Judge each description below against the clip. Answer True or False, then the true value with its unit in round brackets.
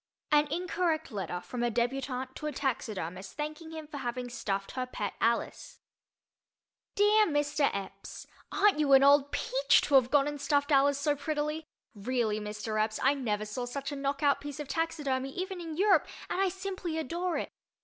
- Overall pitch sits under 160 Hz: False (280 Hz)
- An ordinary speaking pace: True (180 wpm)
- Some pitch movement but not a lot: True (4.4 semitones)